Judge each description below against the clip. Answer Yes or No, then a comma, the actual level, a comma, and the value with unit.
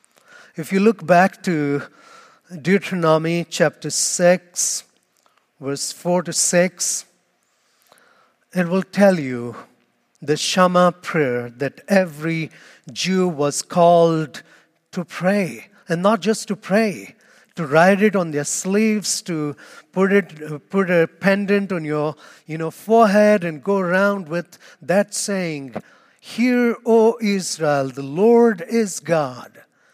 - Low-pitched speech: No, medium, 180 Hz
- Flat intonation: No, average, 4.1 semitones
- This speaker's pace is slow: Yes, slow, 120 wpm